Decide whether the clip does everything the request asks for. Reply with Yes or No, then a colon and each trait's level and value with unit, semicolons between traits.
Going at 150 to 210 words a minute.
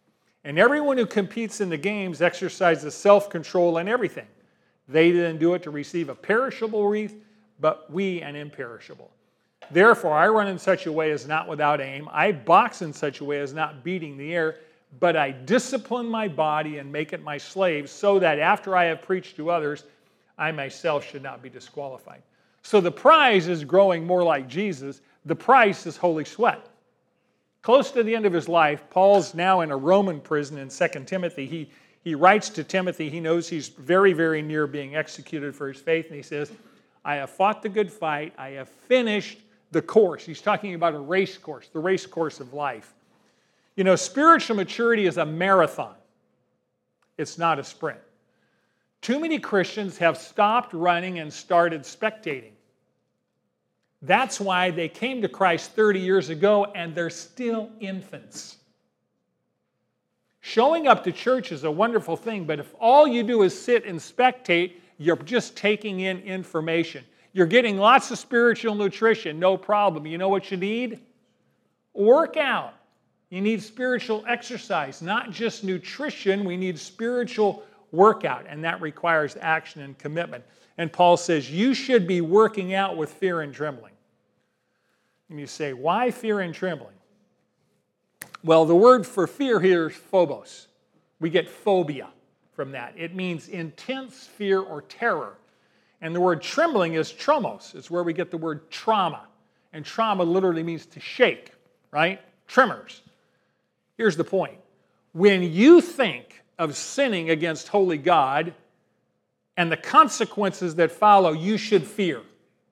Yes: average, 160 wpm